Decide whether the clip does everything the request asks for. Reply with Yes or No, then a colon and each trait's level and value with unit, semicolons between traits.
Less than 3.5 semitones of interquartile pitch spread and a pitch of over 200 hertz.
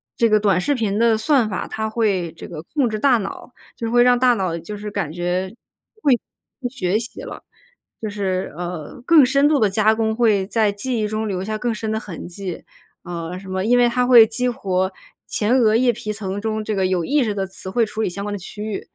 No: average, 3.8 semitones; high, 215 Hz